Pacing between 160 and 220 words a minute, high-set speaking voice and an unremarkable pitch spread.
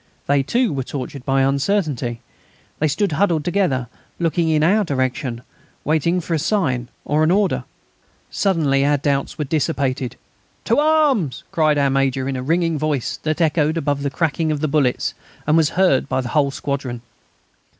No: average, 170 wpm; medium, 150 Hz; average, 3.5 semitones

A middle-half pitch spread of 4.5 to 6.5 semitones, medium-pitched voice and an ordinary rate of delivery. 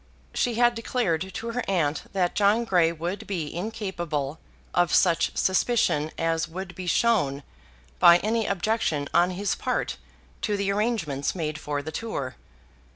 Yes: average, 5.1 semitones; medium, 180 Hz; average, 150 wpm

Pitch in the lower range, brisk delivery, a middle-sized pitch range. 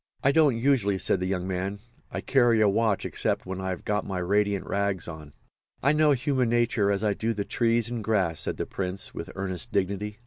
Yes: low, 100 Hz; fast, 210 wpm; average, 3.7 semitones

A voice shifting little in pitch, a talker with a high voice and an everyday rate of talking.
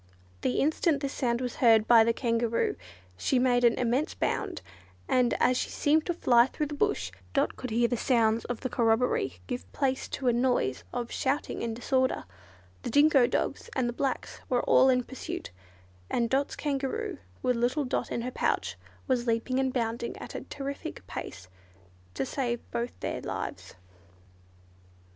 Yes: narrow, 2.3 semitones; very high, 250 Hz; average, 170 wpm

